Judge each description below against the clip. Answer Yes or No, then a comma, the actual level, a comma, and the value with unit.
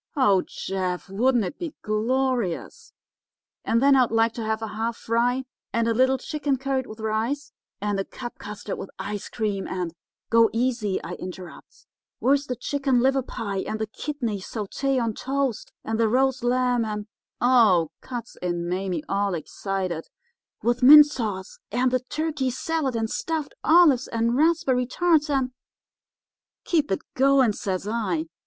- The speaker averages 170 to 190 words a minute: No, average, 160 wpm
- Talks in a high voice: Yes, high, 235 Hz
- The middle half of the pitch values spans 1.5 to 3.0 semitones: No, average, 4.3 semitones